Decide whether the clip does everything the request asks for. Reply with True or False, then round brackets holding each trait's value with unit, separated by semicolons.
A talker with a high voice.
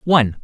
False (135 Hz)